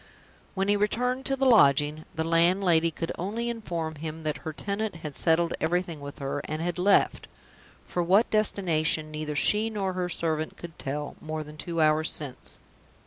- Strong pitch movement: No, average, 4.3 semitones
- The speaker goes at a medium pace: Yes, average, 175 wpm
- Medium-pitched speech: Yes, medium, 165 Hz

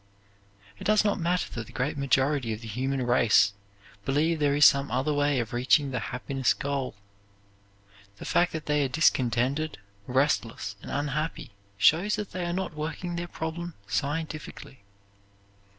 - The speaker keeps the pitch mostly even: No, average, 3.9 semitones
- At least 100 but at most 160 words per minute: Yes, average, 155 wpm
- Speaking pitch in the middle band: Yes, medium, 145 Hz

